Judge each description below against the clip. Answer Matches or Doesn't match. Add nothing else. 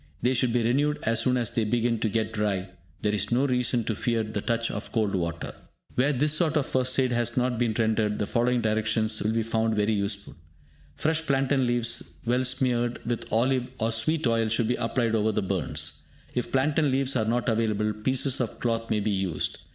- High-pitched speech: Doesn't match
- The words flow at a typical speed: Doesn't match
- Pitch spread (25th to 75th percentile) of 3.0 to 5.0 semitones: Doesn't match